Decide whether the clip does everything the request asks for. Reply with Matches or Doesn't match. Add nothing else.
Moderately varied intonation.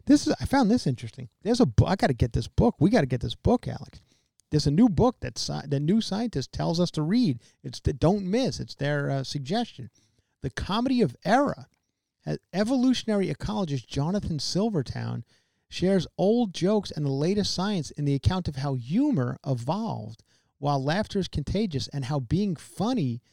Doesn't match